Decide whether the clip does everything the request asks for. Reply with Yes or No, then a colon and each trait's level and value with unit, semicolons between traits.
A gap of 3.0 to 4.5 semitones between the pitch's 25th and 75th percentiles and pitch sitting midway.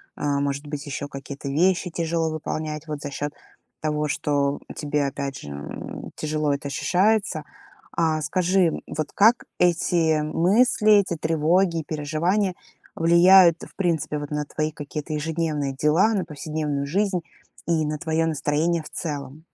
No: narrow, 2.6 semitones; medium, 155 Hz